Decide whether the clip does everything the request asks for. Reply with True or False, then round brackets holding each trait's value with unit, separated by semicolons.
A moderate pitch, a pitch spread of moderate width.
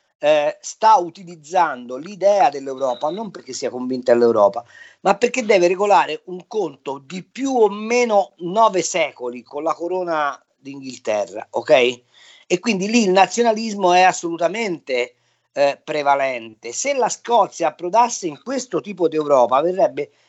False (180 Hz; 7.7 semitones)